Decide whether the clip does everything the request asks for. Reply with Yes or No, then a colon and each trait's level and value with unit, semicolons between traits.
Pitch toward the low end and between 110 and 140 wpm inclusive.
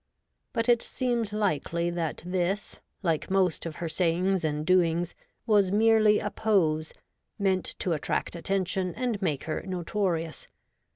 No: medium, 185 Hz; slow, 135 wpm